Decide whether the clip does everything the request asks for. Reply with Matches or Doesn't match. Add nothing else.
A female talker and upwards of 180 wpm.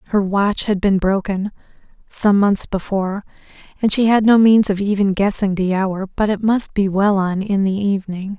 Matches